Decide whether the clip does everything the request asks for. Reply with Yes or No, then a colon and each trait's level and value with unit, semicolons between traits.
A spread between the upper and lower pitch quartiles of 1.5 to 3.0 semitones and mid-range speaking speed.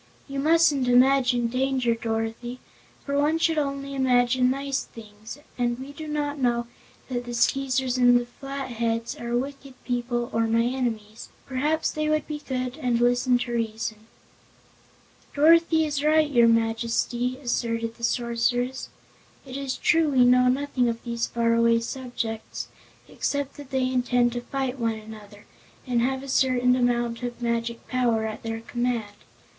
Yes: narrow, 2.6 semitones; average, 150 wpm